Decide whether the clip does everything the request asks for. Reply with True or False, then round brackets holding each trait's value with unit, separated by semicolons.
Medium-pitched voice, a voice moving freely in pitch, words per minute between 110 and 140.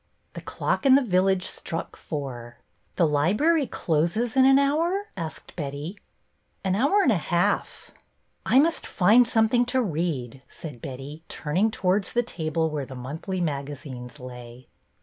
False (175 Hz; 8.2 semitones; 150 wpm)